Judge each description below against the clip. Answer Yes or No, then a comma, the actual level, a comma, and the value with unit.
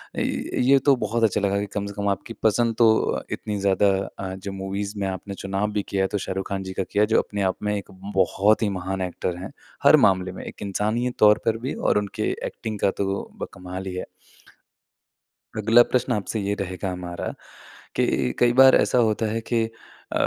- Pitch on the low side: Yes, low, 100 Hz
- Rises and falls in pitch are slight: Yes, narrow, 2.2 semitones